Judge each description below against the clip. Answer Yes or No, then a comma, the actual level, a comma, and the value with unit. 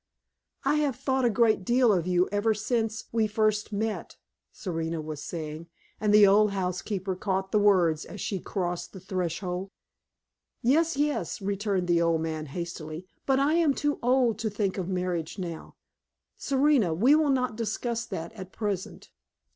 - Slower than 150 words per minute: No, average, 165 wpm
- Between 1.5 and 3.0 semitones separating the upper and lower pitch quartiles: No, average, 4.7 semitones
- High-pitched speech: Yes, high, 200 Hz